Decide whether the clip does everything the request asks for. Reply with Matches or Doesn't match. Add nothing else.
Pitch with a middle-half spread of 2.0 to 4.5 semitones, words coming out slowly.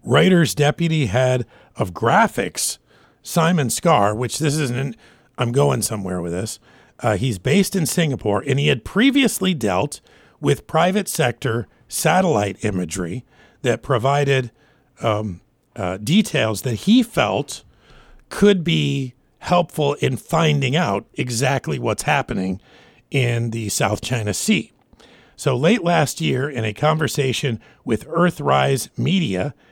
Doesn't match